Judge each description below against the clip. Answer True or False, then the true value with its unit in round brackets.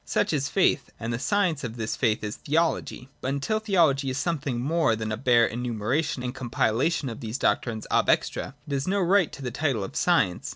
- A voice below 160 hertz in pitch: True (135 Hz)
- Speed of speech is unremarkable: False (215 wpm)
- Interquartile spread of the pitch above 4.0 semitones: True (5.6 semitones)